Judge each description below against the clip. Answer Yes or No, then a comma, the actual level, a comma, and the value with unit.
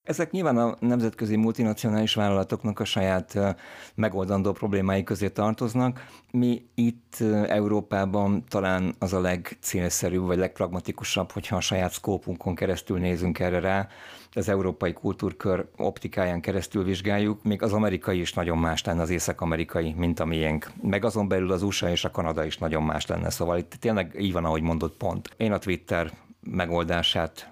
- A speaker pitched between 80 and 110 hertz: Yes, very low, 95 Hz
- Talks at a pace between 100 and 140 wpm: No, fast, 155 wpm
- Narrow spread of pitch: No, average, 3.2 semitones